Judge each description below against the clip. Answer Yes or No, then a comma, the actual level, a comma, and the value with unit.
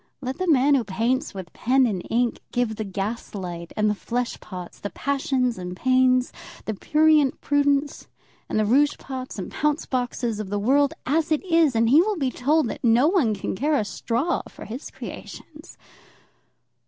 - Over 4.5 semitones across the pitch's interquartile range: Yes, average, 4.9 semitones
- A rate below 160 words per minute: No, average, 185 wpm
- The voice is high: Yes, very high, 255 Hz